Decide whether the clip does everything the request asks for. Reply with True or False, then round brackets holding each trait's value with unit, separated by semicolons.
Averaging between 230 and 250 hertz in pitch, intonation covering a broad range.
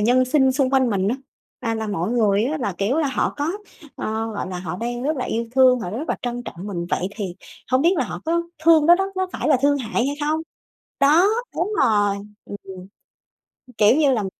True (245 Hz; 5.7 semitones)